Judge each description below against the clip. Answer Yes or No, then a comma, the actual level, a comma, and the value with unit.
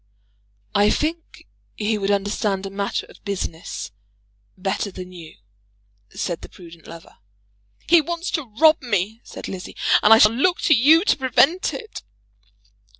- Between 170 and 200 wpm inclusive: No, average, 150 wpm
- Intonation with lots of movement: Yes, wide, 8.1 semitones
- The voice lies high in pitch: Yes, high, 210 Hz